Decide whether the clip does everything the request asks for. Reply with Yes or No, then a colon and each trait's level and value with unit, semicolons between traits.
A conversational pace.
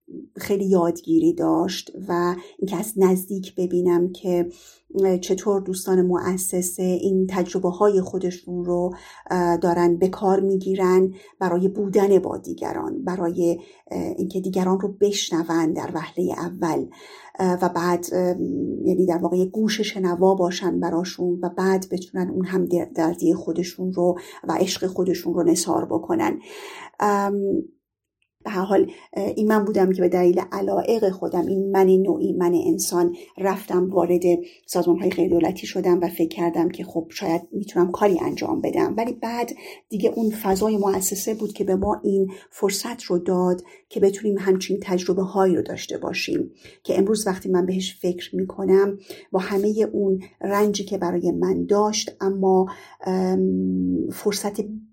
Yes: average, 140 wpm